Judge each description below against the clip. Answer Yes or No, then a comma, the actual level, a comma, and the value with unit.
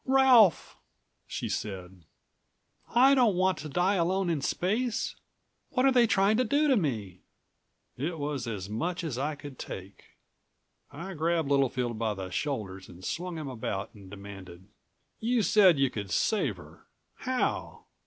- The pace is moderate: Yes, average, 155 wpm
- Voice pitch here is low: No, medium, 150 Hz